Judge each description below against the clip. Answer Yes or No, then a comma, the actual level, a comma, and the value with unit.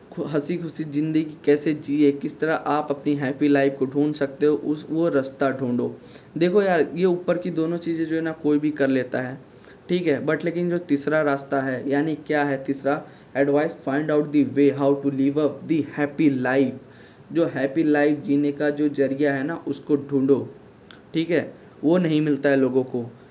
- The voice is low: No, medium, 145 Hz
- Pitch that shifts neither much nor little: No, narrow, 2.2 semitones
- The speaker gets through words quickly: Yes, fast, 200 wpm